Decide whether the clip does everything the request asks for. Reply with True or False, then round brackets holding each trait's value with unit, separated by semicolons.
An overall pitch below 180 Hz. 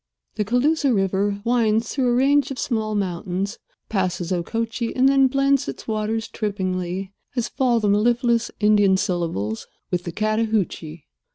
False (215 Hz)